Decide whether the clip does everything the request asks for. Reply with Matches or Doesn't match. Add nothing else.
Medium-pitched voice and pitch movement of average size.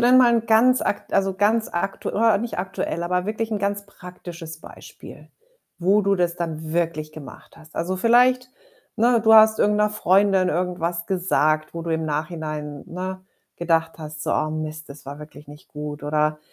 Matches